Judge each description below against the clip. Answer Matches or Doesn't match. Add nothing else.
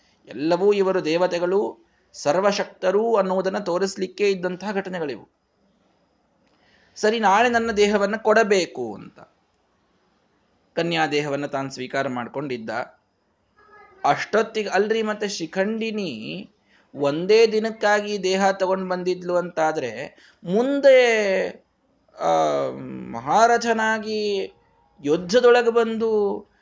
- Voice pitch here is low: Doesn't match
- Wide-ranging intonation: Doesn't match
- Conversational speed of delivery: Matches